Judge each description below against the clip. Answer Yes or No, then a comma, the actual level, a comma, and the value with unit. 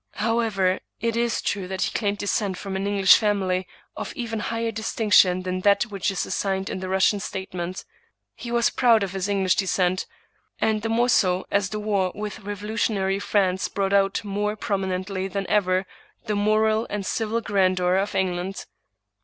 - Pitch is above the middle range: Yes, high, 200 Hz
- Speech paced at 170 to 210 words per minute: Yes, average, 175 wpm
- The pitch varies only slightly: Yes, narrow, 2.2 semitones